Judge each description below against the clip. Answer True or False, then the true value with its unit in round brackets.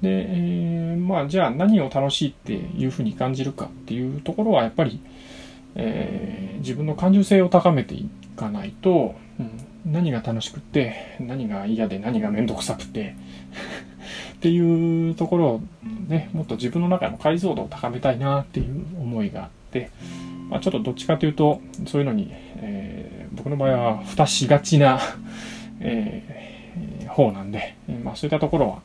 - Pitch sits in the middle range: True (155 Hz)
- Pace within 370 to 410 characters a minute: False (340 characters per minute)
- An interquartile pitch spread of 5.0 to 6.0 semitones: False (8.4 semitones)